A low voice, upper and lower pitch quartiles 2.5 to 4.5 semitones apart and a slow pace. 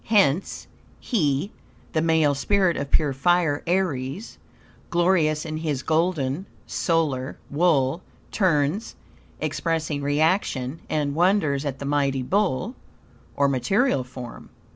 No: medium, 155 Hz; average, 4.2 semitones; slow, 110 wpm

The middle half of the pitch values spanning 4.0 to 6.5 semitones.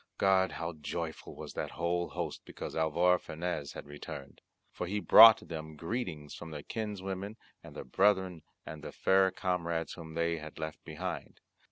No: average, 3.2 semitones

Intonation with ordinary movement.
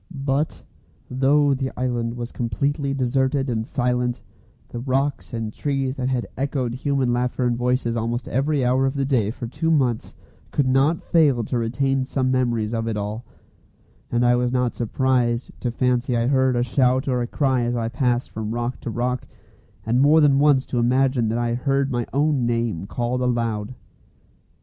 No: narrow, 2.2 semitones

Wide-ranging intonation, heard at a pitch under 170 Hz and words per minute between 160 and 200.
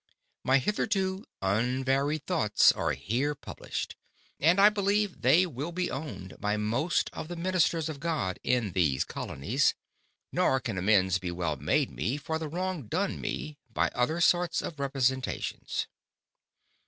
No: wide, 7.9 semitones; medium, 140 Hz; average, 145 wpm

